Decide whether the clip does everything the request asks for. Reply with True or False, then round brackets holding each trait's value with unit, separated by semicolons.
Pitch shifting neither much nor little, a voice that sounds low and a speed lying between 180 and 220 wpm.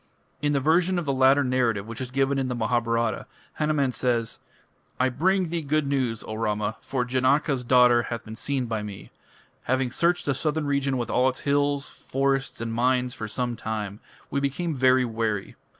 True (3.2 semitones; 130 Hz; 185 wpm)